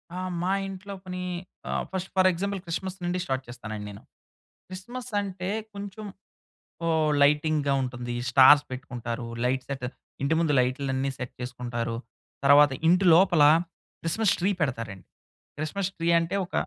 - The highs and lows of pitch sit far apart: Yes, wide, 6.6 semitones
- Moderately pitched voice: Yes, medium, 150 Hz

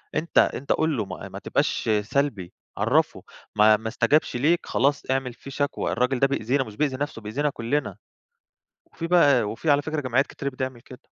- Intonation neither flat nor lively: Yes, average, 3.8 semitones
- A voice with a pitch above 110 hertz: Yes, low, 135 Hz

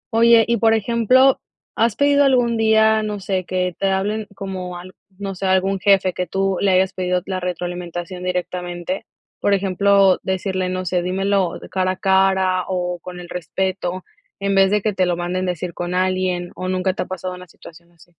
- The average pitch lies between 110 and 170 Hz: No, medium, 185 Hz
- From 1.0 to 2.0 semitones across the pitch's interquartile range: Yes, narrow, 1.7 semitones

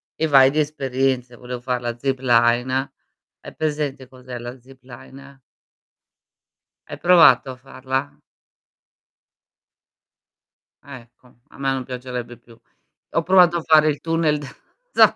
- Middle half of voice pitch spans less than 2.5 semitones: No, average, 2.8 semitones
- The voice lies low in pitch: Yes, low, 130 Hz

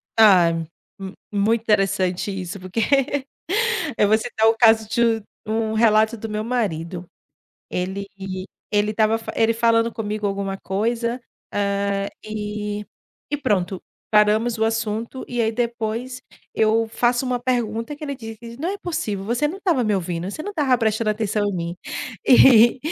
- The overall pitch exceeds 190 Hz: Yes, high, 220 Hz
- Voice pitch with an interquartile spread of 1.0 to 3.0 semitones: Yes, narrow, 2.5 semitones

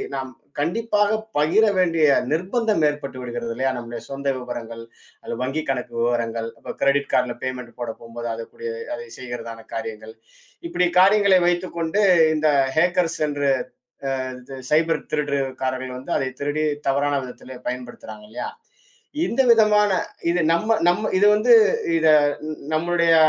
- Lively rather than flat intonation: Yes, wide, 6.2 semitones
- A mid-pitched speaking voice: Yes, medium, 145 Hz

